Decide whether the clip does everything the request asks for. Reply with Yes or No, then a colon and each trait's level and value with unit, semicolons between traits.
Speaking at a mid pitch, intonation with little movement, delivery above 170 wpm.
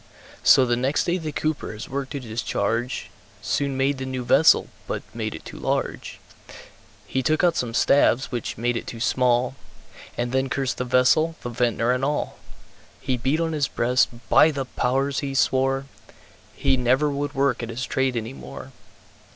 No: low, 130 Hz; narrow, 2.3 semitones; average, 180 wpm